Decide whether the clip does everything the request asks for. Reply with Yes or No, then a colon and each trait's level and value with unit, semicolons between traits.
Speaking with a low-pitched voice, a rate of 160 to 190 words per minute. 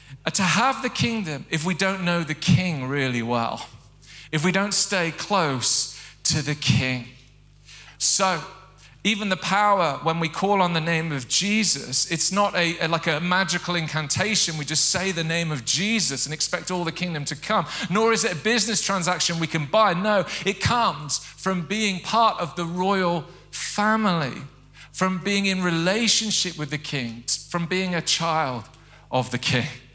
No: medium, 170 Hz; average, 170 wpm